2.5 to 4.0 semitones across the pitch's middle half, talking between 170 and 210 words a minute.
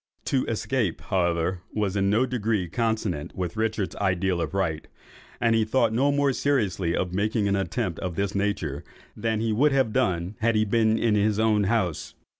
Yes: average, 3.6 semitones; average, 185 wpm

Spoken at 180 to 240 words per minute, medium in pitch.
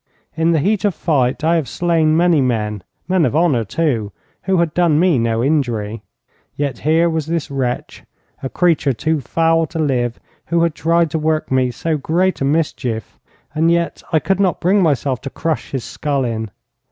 Yes: average, 190 wpm; medium, 155 Hz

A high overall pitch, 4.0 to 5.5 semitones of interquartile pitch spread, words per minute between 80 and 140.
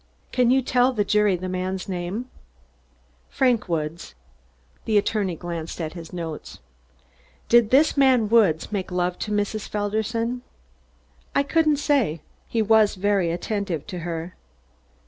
Yes: high, 205 Hz; average, 4.9 semitones; slow, 135 wpm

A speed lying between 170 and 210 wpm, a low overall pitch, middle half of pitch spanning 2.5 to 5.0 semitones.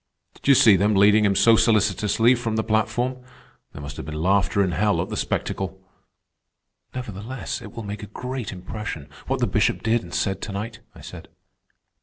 Yes: average, 190 wpm; low, 105 Hz; average, 2.9 semitones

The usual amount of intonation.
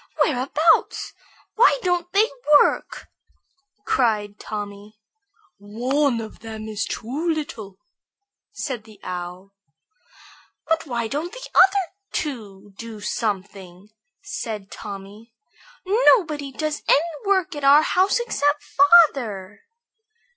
No: wide, 7.7 semitones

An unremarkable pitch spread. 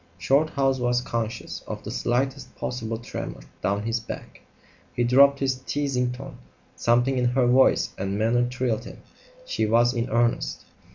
No: narrow, 2.1 semitones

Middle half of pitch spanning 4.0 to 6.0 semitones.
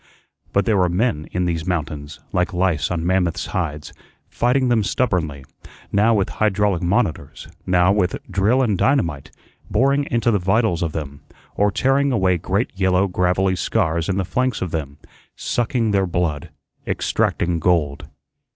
Yes: average, 4.3 semitones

